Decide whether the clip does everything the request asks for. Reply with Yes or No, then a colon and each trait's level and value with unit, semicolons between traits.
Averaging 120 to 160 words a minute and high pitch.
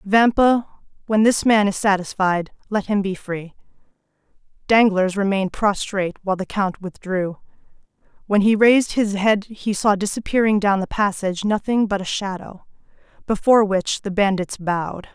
Yes: average, 145 wpm; high, 200 Hz